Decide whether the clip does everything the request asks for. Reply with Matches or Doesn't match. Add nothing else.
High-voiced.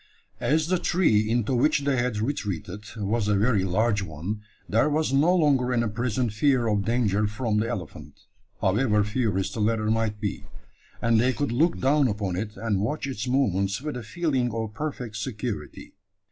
Doesn't match